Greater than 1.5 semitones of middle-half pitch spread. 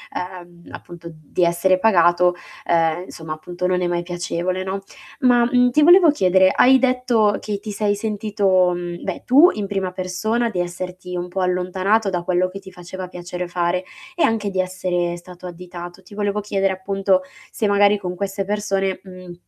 Yes: narrow, 2.5 semitones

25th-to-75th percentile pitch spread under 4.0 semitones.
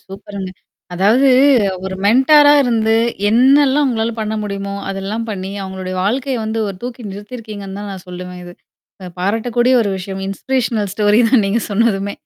Yes: average, 3.6 semitones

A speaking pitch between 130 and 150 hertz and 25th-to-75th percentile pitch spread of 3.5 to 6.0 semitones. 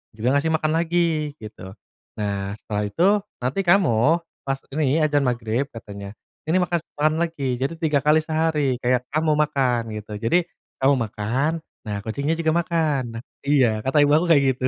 Yes: medium, 140 Hz; average, 4.7 semitones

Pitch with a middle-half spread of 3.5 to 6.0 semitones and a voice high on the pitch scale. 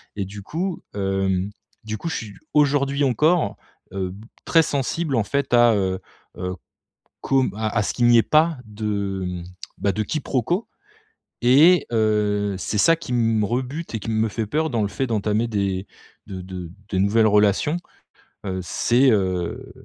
No: average, 5.3 semitones; low, 110 Hz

